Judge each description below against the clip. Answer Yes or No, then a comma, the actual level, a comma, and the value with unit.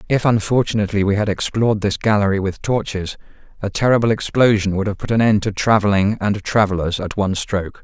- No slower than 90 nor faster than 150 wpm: No, average, 185 wpm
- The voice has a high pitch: No, low, 105 Hz